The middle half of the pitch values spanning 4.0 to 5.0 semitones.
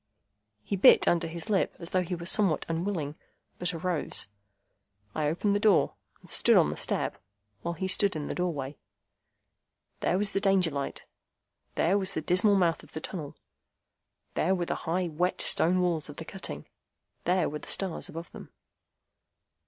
No: average, 2.9 semitones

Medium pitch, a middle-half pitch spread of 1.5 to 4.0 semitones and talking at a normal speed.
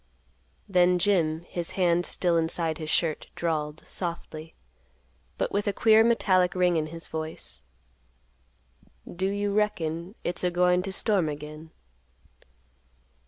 No: medium, 175 Hz; average, 2.9 semitones; slow, 125 wpm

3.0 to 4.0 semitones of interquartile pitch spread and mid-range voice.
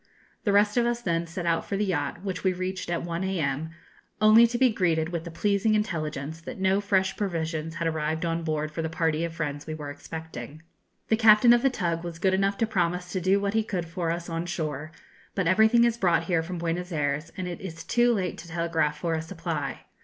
Yes: average, 3.3 semitones; medium, 170 Hz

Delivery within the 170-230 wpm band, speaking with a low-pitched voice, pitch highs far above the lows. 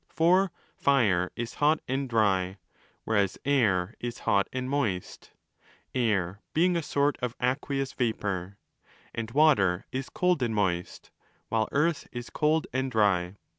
No: slow, 135 wpm; low, 120 Hz; wide, 6.2 semitones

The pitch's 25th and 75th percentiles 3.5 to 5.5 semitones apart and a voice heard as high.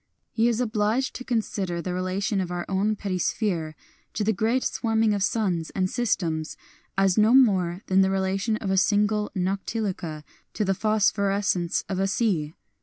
No: average, 2.9 semitones; high, 195 Hz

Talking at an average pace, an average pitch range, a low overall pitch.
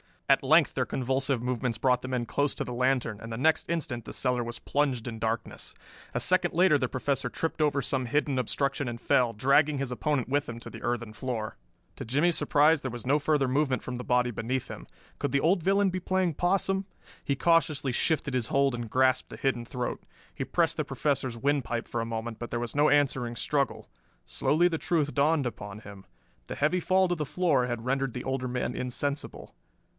No: fast, 210 wpm; average, 3.4 semitones; low, 130 Hz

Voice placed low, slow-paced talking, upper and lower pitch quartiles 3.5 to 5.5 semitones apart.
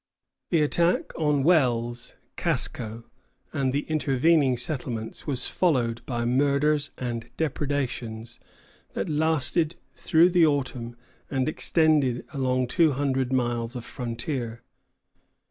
Yes: low, 130 Hz; slow, 110 wpm; average, 4.1 semitones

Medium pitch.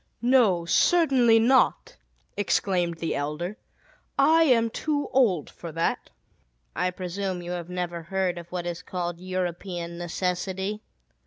Yes: medium, 180 Hz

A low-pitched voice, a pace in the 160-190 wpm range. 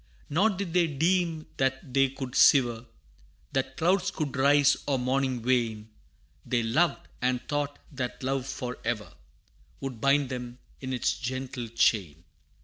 No: low, 130 Hz; average, 140 wpm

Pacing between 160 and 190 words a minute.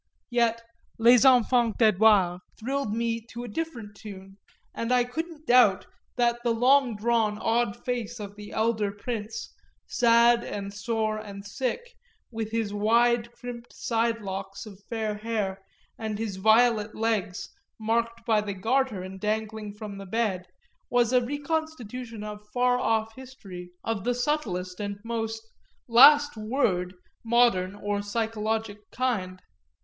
No: average, 140 wpm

